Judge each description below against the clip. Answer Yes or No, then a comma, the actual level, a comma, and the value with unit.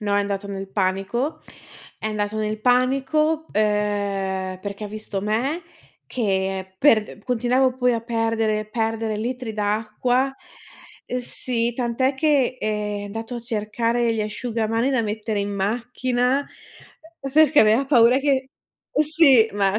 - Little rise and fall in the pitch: No, average, 3.3 semitones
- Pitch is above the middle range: Yes, high, 225 Hz